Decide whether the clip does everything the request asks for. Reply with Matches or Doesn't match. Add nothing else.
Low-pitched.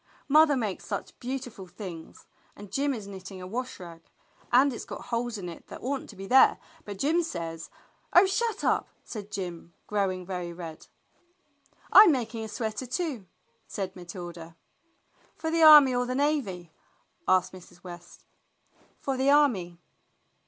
Doesn't match